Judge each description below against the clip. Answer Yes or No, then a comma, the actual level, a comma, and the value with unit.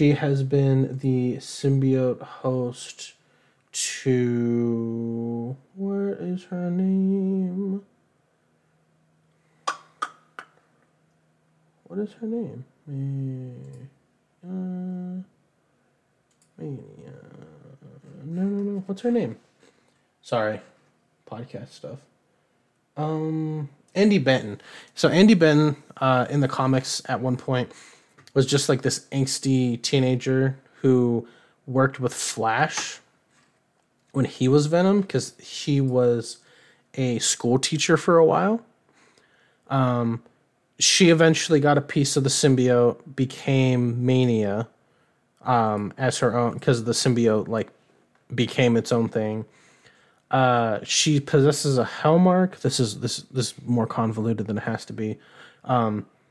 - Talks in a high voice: No, low, 135 Hz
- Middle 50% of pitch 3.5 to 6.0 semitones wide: Yes, average, 4.4 semitones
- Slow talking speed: Yes, slow, 110 wpm